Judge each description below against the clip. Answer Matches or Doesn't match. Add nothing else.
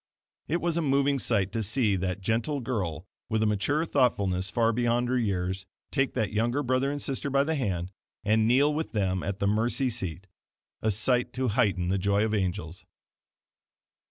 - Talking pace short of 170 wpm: Doesn't match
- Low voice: Matches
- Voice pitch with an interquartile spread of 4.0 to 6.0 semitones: Matches